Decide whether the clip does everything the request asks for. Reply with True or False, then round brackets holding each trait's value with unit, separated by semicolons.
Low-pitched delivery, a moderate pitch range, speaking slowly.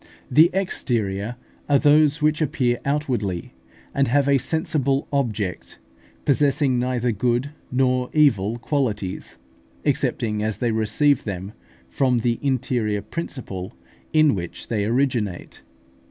True (125 Hz; 4.8 semitones; 115 wpm)